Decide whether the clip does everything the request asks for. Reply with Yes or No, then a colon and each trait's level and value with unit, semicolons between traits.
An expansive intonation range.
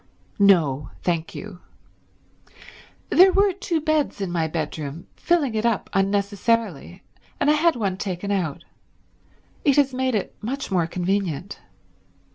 Yes: wide, 7.6 semitones